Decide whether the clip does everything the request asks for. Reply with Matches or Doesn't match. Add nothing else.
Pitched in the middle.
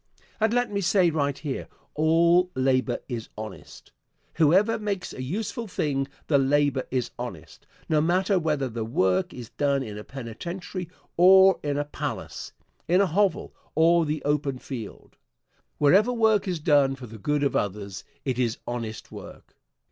Matches